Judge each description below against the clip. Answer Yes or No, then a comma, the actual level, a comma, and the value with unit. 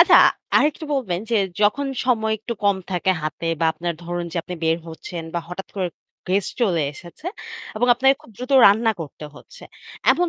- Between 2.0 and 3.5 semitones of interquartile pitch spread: No, wide, 5.6 semitones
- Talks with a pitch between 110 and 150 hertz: No, high, 195 Hz